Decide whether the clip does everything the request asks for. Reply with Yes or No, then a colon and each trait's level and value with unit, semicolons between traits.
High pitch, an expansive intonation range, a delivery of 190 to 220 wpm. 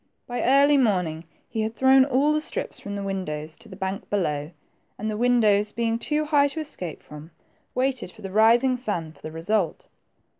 Yes: high, 215 Hz; wide, 5.9 semitones; average, 195 wpm